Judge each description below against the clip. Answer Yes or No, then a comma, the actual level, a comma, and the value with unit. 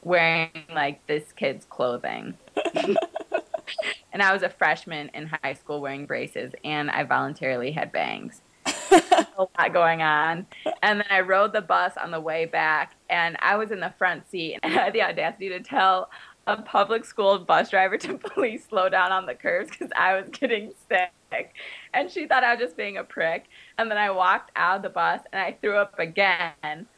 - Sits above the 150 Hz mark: Yes, medium, 185 Hz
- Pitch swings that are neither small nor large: Yes, average, 4.6 semitones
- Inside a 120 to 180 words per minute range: No, average, 195 wpm